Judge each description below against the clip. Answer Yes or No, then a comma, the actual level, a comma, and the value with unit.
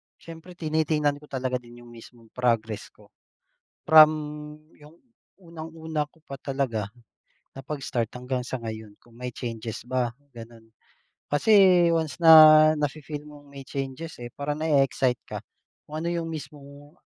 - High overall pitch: No, medium, 140 Hz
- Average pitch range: Yes, average, 4.2 semitones